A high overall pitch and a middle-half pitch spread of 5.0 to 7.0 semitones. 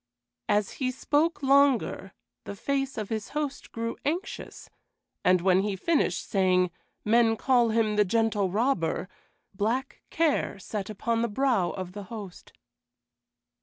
Yes: high, 225 Hz; wide, 5.4 semitones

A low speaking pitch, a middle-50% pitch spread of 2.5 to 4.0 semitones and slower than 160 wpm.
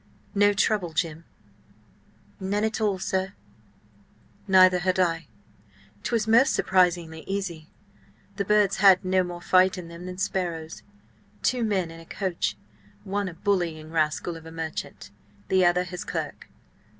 No: medium, 185 Hz; average, 2.9 semitones; average, 140 wpm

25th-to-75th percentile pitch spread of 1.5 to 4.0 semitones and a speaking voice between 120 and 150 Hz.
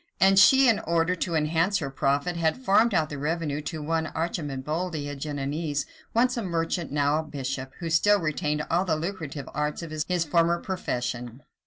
No: average, 3.4 semitones; medium, 160 Hz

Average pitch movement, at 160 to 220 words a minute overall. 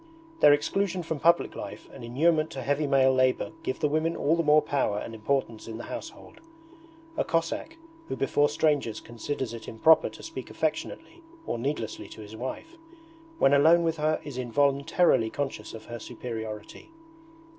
Yes: average, 5.0 semitones; average, 165 wpm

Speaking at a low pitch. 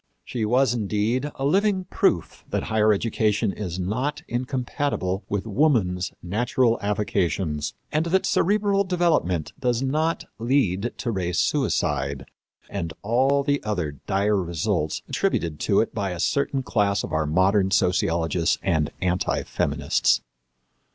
Yes: low, 105 Hz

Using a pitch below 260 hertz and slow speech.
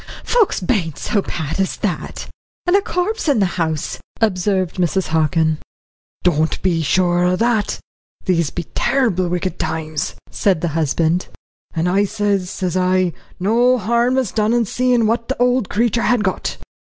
No: high, 190 Hz; average, 160 wpm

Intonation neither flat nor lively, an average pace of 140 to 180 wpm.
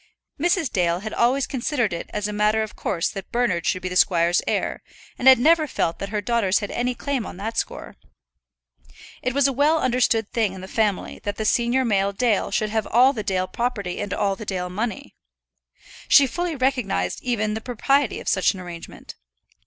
No: average, 4.6 semitones; average, 200 wpm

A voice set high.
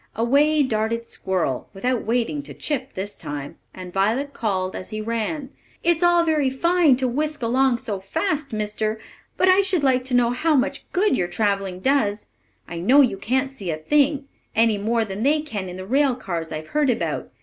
Yes: high, 245 Hz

